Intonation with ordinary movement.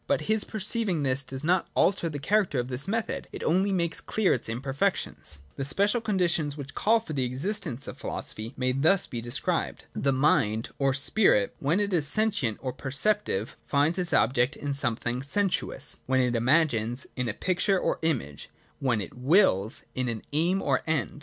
No: wide, 6.8 semitones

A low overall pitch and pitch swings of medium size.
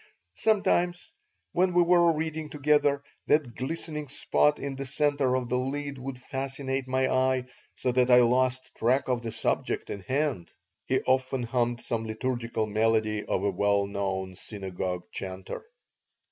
Yes: low, 130 Hz; average, 4.2 semitones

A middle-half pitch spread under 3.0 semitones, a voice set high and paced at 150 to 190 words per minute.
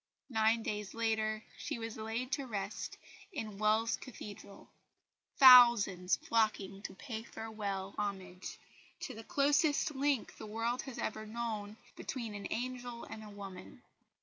No: narrow, 2.6 semitones; high, 220 Hz; slow, 135 wpm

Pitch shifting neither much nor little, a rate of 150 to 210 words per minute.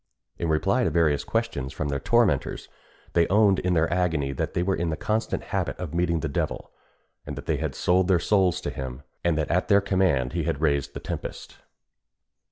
Yes: average, 4.1 semitones; average, 200 wpm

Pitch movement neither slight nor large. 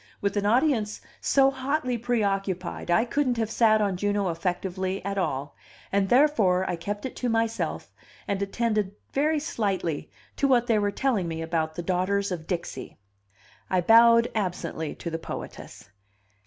Yes: average, 4.5 semitones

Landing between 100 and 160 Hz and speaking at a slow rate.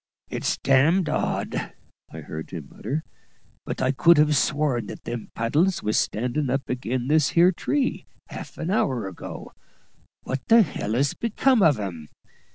No: low, 135 Hz; average, 165 wpm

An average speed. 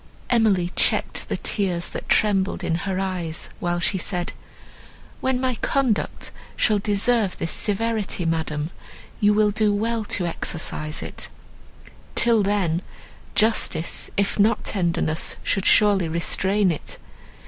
No: slow, 125 wpm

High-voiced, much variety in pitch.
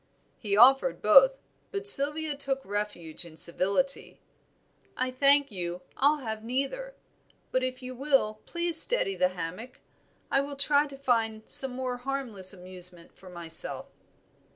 Yes: very high, 255 Hz; wide, 6.3 semitones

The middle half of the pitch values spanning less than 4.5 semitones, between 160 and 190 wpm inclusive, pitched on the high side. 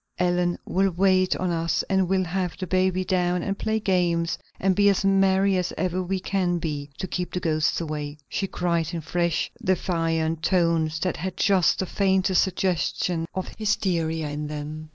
No: narrow, 2.4 semitones; average, 175 wpm; medium, 180 Hz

